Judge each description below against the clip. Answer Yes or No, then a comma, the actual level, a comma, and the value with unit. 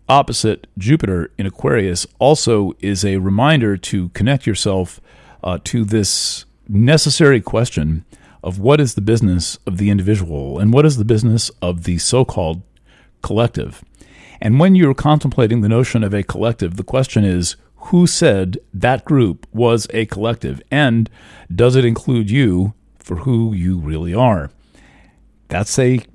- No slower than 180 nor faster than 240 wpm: No, average, 150 wpm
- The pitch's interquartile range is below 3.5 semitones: No, average, 4.6 semitones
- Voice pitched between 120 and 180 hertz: No, low, 110 Hz